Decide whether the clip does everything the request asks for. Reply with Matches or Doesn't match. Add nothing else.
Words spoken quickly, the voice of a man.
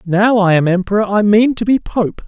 Matches